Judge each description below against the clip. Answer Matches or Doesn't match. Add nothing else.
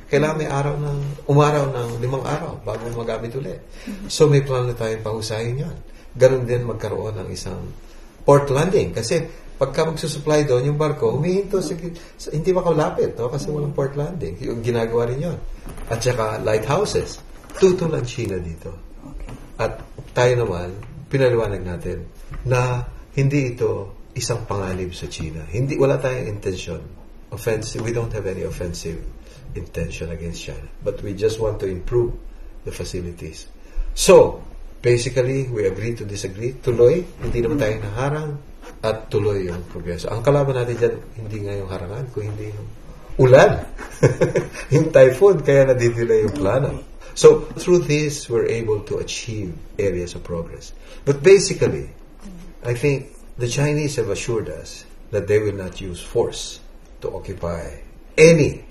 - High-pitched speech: Doesn't match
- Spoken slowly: Doesn't match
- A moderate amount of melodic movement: Doesn't match